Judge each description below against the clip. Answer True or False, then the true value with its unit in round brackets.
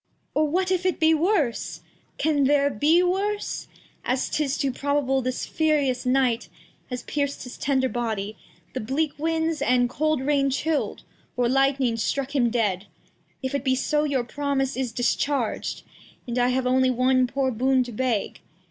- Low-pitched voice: False (270 Hz)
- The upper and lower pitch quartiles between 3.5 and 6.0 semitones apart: False (2.9 semitones)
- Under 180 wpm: True (150 wpm)